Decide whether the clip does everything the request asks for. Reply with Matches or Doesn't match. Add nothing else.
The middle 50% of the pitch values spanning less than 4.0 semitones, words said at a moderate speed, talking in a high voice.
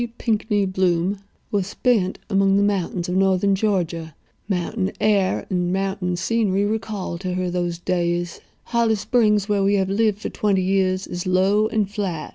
Matches